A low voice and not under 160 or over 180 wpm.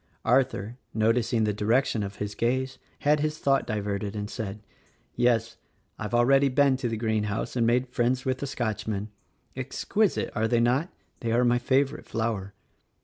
Yes: low, 120 Hz; average, 165 wpm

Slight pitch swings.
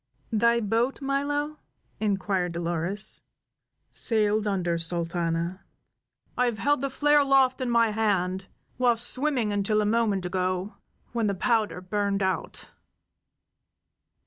No: average, 4.5 semitones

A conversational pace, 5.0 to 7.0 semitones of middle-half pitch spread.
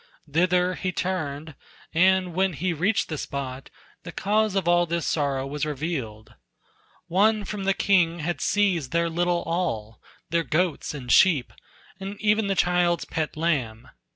No: average, 155 wpm; average, 3.9 semitones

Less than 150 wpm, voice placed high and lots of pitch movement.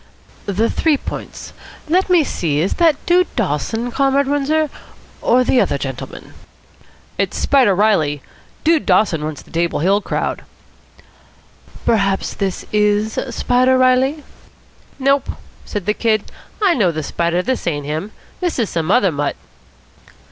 Yes: average, 140 wpm; high, 215 Hz; wide, 7.7 semitones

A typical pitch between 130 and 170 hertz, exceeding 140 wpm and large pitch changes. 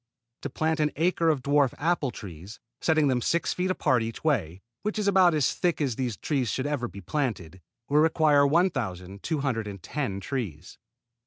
Yes: medium, 140 Hz; average, 165 wpm; wide, 6.7 semitones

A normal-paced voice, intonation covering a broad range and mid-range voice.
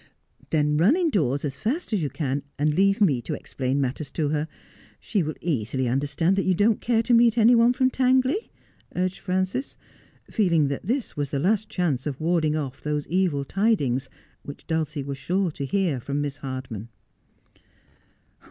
Yes: average, 180 wpm; wide, 6.3 semitones; medium, 155 Hz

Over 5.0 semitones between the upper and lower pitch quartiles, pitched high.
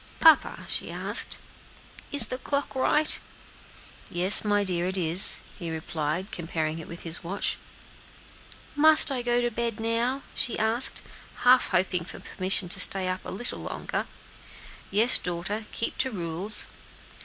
Yes: wide, 5.6 semitones; high, 205 Hz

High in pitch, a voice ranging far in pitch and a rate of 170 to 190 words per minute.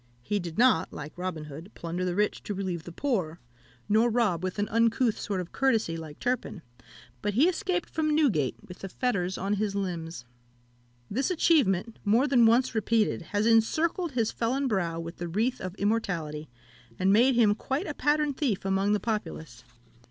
Yes: high, 210 Hz; wide, 5.7 semitones; average, 180 wpm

